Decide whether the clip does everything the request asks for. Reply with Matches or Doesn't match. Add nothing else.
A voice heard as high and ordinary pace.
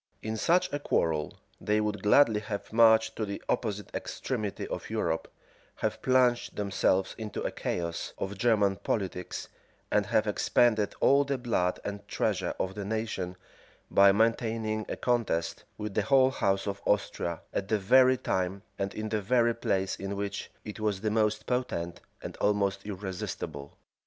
Doesn't match